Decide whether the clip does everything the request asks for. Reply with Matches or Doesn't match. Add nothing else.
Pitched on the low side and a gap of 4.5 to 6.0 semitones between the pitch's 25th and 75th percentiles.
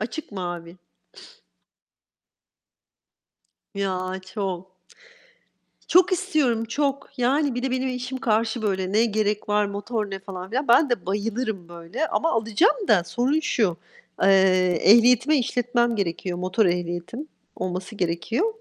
Doesn't match